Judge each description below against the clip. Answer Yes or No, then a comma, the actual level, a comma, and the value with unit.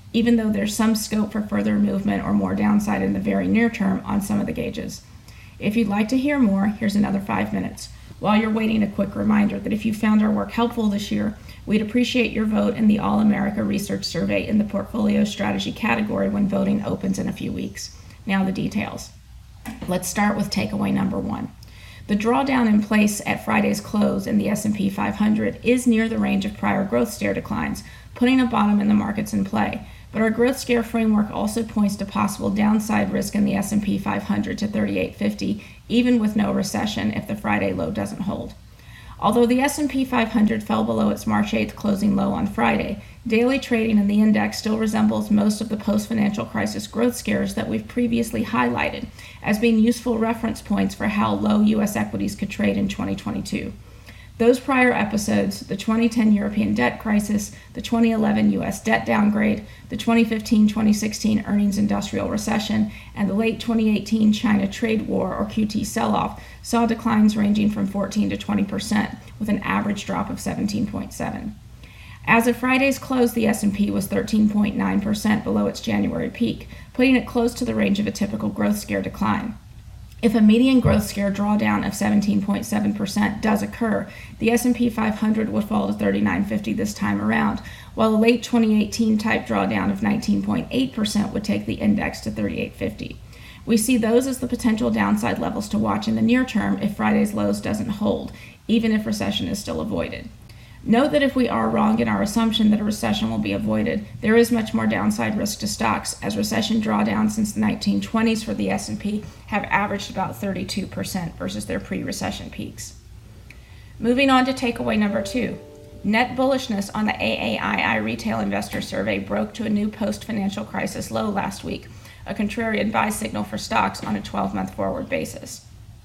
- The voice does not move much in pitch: Yes, narrow, 1.9 semitones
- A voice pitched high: Yes, high, 215 Hz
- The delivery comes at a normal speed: Yes, average, 180 wpm